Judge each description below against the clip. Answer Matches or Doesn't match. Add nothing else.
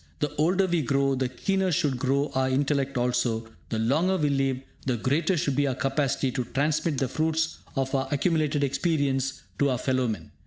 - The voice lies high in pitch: Doesn't match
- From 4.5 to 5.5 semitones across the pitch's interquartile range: Doesn't match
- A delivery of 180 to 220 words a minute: Matches